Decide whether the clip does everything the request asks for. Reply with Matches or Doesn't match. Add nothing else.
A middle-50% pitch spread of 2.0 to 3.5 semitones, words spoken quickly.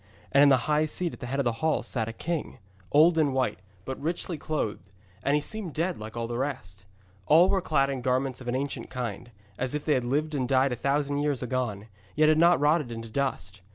Doesn't match